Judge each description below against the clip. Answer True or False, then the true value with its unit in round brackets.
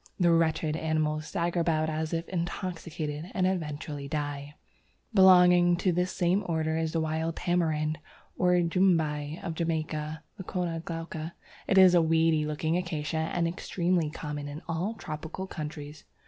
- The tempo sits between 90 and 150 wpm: True (145 wpm)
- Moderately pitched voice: True (165 Hz)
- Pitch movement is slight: True (2.2 semitones)